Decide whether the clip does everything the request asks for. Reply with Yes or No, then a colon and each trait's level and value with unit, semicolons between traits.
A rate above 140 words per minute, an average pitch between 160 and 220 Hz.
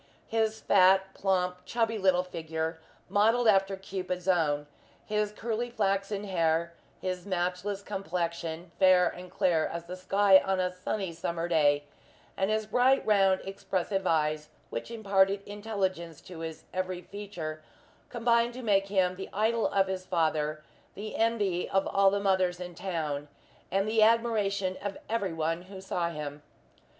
Yes: average, 150 wpm; high, 190 Hz